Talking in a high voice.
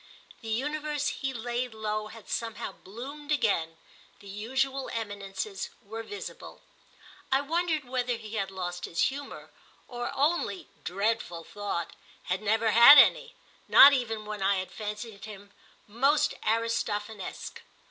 Yes: high, 225 Hz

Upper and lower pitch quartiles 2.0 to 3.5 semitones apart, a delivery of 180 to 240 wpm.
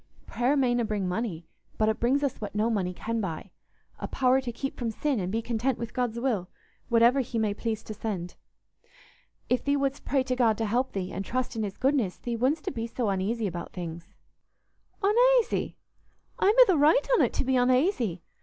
No: average, 4.1 semitones; average, 195 wpm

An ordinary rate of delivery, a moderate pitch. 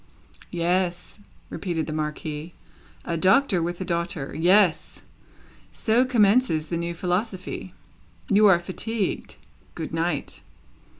No: slow, 110 wpm; medium, 175 Hz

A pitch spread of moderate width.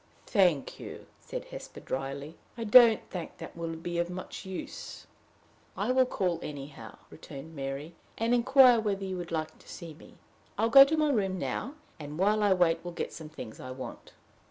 No: wide, 5.9 semitones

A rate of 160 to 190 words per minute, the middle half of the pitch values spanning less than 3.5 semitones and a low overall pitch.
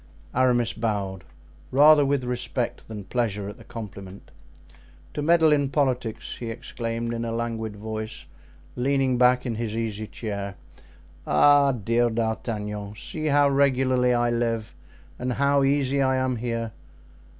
No: average, 140 wpm; average, 3.1 semitones; low, 120 Hz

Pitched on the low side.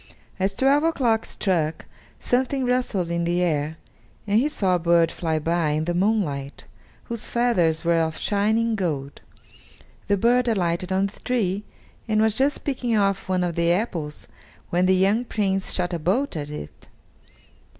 No: high, 190 Hz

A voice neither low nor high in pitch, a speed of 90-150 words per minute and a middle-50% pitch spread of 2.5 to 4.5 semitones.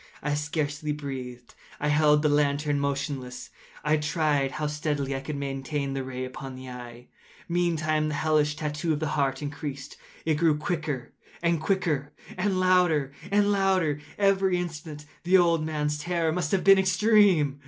No: medium, 150 Hz; average, 160 wpm; average, 3.0 semitones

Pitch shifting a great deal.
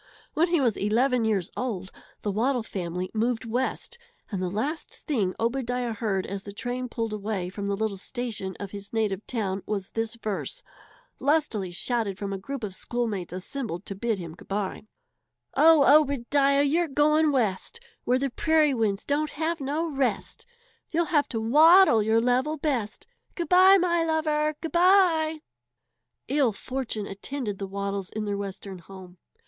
Yes: wide, 6.5 semitones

